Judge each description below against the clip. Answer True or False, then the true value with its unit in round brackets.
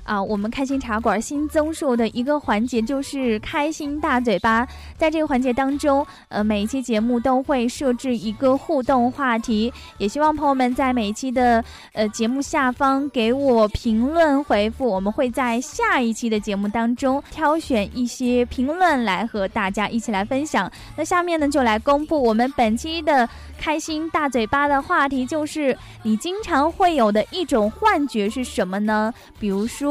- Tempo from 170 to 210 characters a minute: False (270 characters per minute)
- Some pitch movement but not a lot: True (4.3 semitones)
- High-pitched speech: True (255 Hz)